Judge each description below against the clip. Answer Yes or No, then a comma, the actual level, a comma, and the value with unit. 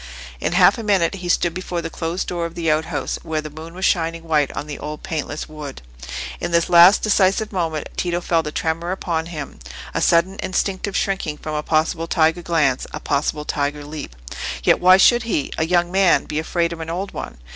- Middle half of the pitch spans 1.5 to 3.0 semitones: Yes, narrow, 2.6 semitones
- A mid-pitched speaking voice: Yes, medium, 165 Hz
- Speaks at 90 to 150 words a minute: No, fast, 205 wpm